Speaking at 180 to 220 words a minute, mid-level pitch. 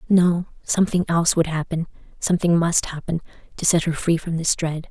No: average, 160 wpm; medium, 165 Hz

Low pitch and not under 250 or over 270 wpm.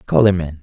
No: very low, 85 Hz; fast, 290 wpm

